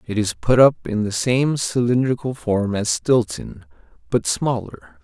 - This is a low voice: Yes, low, 115 Hz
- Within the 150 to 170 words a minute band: Yes, average, 155 wpm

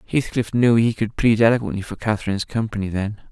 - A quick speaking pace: No, average, 180 wpm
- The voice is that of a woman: No, male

